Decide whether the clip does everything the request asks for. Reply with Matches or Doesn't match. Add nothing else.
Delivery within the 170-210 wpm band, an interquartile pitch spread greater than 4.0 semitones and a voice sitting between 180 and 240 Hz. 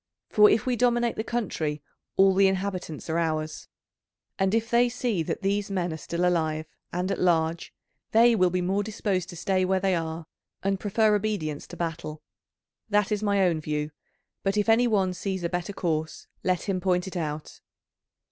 Doesn't match